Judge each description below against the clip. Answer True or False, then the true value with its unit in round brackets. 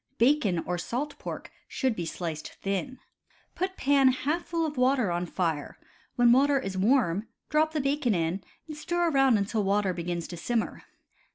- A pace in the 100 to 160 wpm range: False (170 wpm)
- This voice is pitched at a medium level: False (240 Hz)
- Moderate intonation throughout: False (7.6 semitones)